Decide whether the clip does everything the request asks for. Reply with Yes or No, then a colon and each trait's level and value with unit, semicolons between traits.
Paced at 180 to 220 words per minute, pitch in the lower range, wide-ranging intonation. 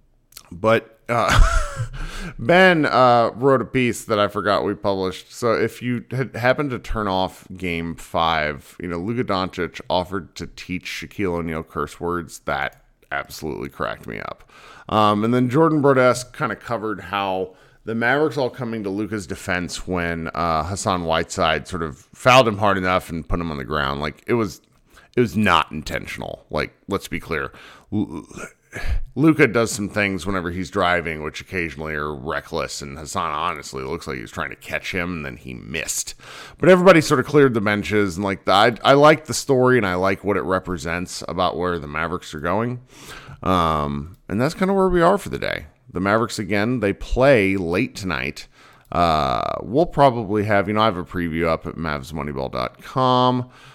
Yes: average, 185 wpm; low, 100 Hz; wide, 6.3 semitones